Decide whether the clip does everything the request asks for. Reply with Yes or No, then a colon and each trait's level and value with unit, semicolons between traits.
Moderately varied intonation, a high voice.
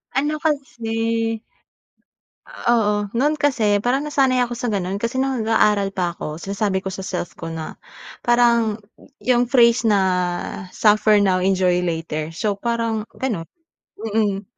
Yes: average, 3.7 semitones; high, 220 Hz